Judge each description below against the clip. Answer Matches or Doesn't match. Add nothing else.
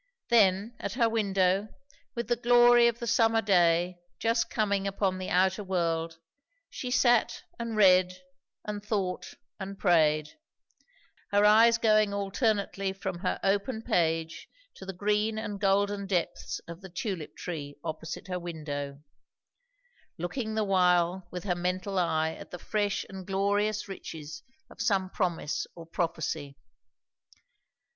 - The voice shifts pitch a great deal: Doesn't match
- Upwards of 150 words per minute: Doesn't match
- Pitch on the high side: Matches